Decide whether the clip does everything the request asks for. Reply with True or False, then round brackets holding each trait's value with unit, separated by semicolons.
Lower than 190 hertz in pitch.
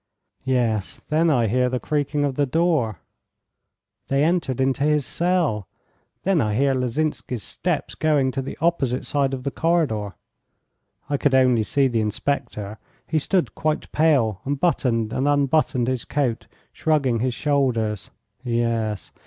True (135 Hz)